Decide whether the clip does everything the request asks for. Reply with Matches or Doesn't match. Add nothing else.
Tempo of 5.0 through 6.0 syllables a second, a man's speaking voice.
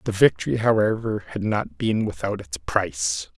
Doesn't match